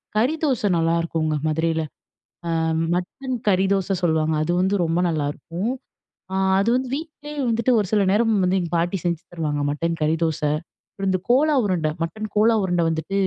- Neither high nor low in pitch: Yes, medium, 180 Hz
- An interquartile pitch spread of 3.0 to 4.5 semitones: No, average, 5.0 semitones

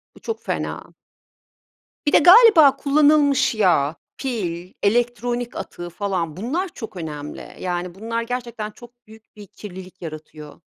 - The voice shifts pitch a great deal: Yes, wide, 5.9 semitones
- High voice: Yes, high, 220 Hz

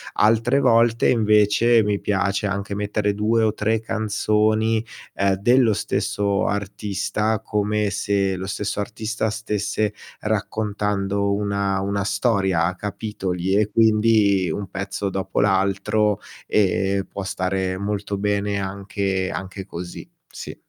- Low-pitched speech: Yes, low, 100 Hz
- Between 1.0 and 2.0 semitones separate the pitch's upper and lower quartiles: Yes, narrow, 1.6 semitones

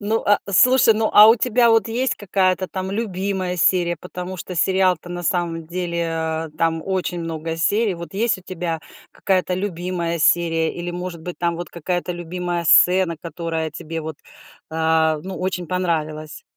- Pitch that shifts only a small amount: Yes, narrow, 2.3 semitones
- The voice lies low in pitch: No, medium, 175 Hz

